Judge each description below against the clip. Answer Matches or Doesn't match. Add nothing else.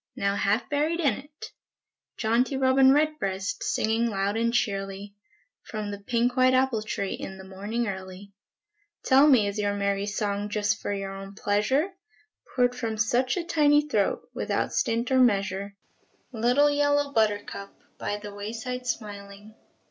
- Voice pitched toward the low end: Doesn't match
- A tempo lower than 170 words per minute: Matches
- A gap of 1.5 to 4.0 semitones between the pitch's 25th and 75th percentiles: Doesn't match